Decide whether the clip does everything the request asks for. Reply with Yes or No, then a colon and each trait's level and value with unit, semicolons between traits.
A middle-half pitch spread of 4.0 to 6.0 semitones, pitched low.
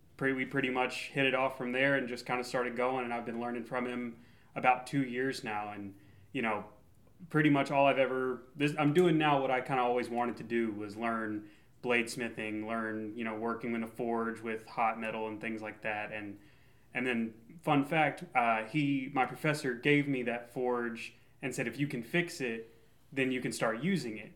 No: average, 2.8 semitones; low, 125 Hz